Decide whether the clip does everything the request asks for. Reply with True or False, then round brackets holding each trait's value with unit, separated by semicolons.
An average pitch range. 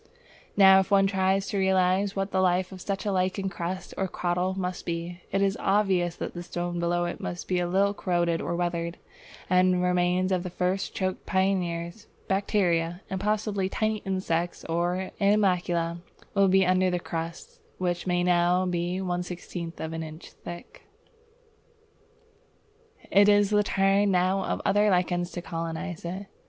False (1.8 semitones)